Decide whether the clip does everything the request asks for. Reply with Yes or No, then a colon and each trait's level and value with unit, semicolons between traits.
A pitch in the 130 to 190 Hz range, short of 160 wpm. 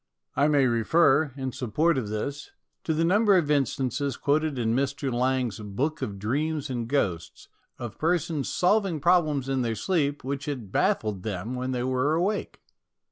No: medium, 140 Hz; average, 170 wpm